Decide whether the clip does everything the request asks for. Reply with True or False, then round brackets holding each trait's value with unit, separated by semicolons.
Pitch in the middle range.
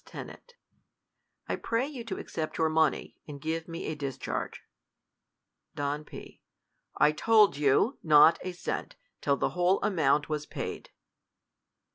True (155 Hz)